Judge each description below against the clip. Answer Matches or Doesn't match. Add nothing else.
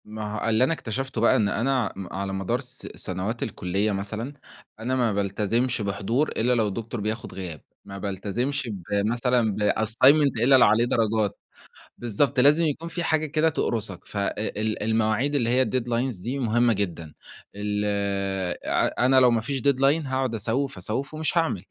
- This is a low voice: Matches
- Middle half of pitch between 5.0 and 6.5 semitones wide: Doesn't match